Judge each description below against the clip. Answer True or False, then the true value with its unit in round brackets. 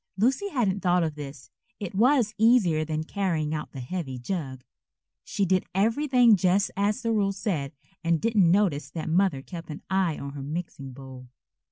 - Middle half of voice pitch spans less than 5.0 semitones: False (5.4 semitones)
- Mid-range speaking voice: True (180 Hz)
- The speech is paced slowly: False (175 wpm)